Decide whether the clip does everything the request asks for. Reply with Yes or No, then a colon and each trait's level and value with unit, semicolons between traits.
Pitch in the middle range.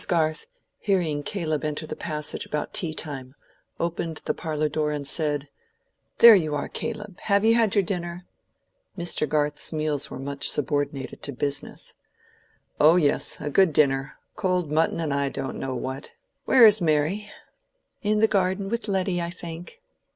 Yes: medium, 155 Hz